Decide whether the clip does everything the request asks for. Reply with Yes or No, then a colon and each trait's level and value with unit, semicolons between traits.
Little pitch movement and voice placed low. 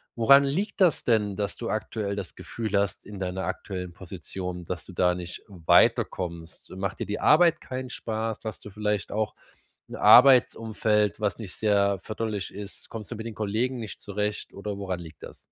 No: average, 3.0 semitones; low, 105 Hz